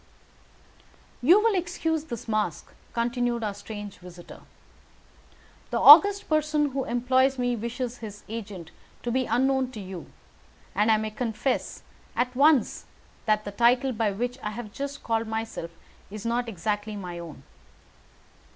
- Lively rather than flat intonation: No, average, 3.8 semitones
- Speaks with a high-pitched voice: Yes, high, 235 Hz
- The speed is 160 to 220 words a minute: No, average, 140 wpm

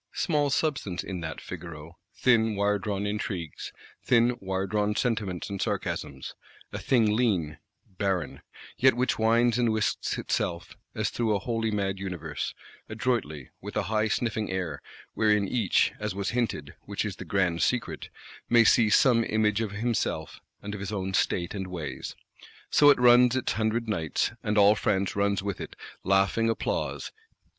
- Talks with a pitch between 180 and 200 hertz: No, low, 105 Hz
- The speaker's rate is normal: Yes, average, 155 wpm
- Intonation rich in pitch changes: No, average, 3.5 semitones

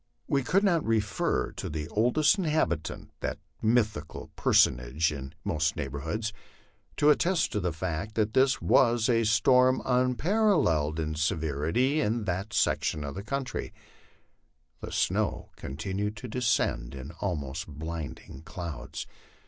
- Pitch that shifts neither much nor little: No, wide, 8.4 semitones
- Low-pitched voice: Yes, low, 105 Hz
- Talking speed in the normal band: No, slow, 130 wpm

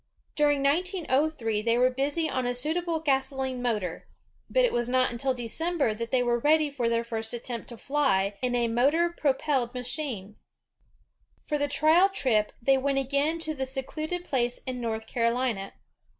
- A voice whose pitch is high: Yes, very high, 260 Hz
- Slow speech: No, average, 165 wpm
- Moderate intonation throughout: Yes, average, 3.9 semitones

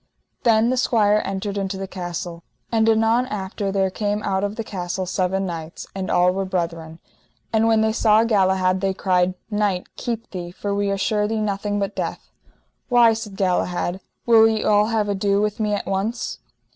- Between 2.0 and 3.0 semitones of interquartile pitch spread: Yes, narrow, 2.5 semitones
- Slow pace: No, average, 185 wpm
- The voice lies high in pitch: Yes, high, 200 Hz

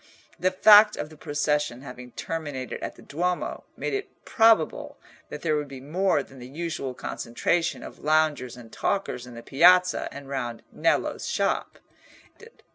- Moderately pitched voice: Yes, medium, 150 Hz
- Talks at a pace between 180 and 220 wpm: No, average, 155 wpm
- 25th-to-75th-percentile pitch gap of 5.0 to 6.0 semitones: Yes, average, 5.3 semitones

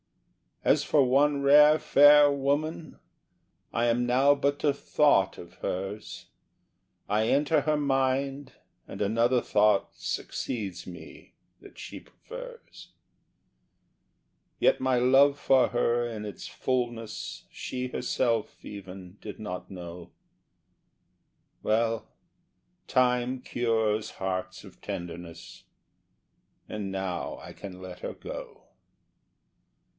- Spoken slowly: Yes, slow, 105 wpm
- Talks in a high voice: No, low, 120 Hz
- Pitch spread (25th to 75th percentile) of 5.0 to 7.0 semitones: Yes, wide, 5.4 semitones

